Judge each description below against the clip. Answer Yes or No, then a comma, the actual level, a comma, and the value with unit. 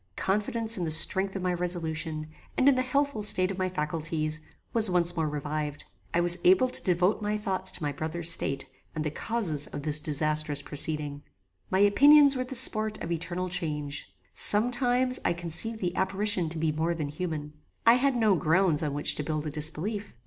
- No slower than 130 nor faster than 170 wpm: No, average, 195 wpm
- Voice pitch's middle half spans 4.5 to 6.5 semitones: Yes, wide, 5.4 semitones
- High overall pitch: No, medium, 175 Hz